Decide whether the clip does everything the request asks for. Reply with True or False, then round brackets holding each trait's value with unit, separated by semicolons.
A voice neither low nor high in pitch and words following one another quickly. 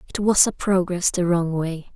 True (180 Hz; 215 wpm)